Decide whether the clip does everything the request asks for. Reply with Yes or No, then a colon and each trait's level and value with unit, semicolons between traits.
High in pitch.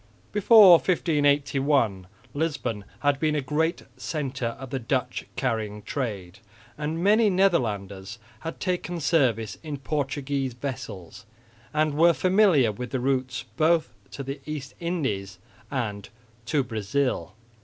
No: medium, 140 Hz